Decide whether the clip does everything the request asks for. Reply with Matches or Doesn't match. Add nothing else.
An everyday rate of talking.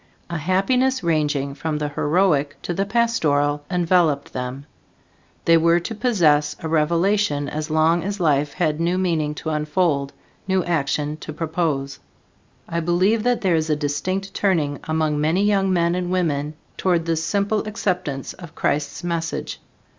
Matches